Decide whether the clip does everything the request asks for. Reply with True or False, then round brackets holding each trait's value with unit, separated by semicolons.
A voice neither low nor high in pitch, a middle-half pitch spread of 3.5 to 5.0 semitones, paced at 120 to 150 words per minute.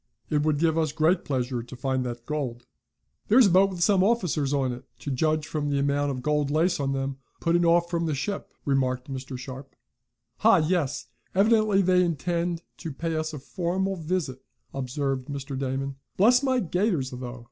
False (150 Hz; 4.6 semitones; 185 wpm)